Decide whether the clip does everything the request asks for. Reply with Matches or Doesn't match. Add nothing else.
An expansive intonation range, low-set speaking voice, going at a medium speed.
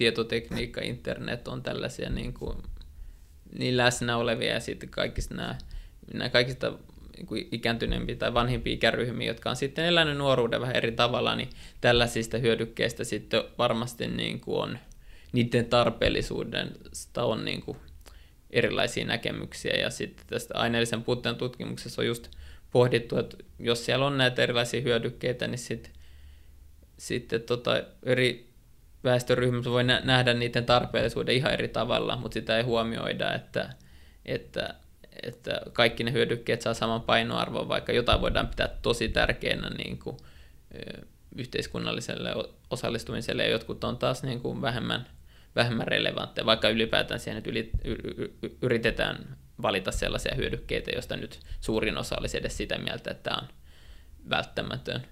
Matches